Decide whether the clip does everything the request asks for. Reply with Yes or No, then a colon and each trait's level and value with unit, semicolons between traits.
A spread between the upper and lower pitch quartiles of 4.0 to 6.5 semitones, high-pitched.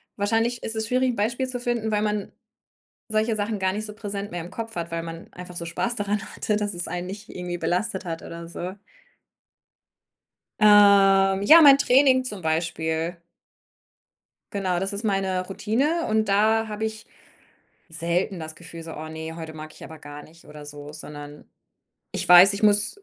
Yes: average, 4.4 semitones; high, 195 Hz